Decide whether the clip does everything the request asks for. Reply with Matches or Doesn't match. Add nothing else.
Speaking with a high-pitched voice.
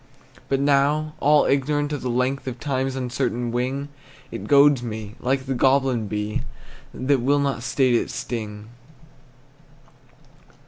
Doesn't match